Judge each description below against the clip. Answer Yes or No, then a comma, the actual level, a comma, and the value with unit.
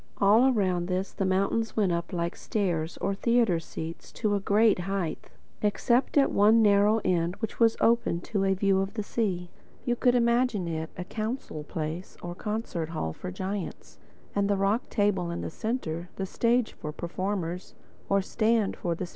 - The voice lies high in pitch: Yes, high, 195 Hz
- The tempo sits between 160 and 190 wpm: Yes, average, 180 wpm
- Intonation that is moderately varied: Yes, average, 4.1 semitones